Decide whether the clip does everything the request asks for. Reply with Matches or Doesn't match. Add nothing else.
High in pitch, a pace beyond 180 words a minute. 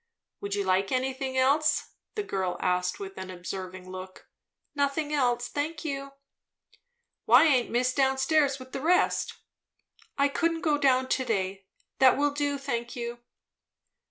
Doesn't match